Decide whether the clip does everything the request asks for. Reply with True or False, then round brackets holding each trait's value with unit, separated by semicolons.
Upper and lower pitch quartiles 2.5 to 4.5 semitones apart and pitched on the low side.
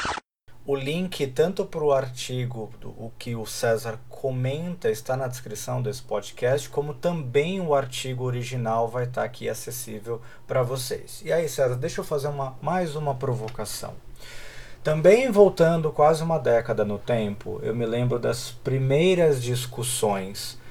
True (4.0 semitones; 130 Hz)